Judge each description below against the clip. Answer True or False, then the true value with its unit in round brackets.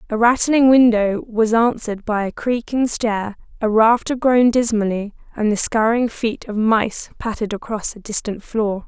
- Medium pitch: False (225 Hz)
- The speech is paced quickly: False (160 wpm)